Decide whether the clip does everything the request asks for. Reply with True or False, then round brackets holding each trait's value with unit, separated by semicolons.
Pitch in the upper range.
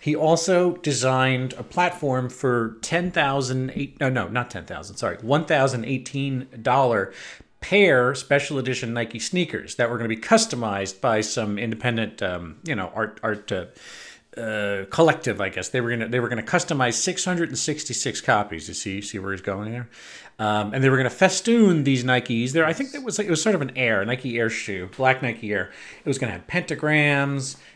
False (125 Hz)